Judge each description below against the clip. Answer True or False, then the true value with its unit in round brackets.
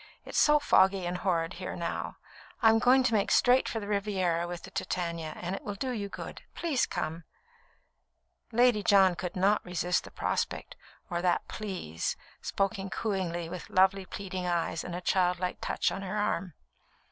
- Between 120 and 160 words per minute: False (170 wpm)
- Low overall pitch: False (190 Hz)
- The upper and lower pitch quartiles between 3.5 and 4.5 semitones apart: False (3.0 semitones)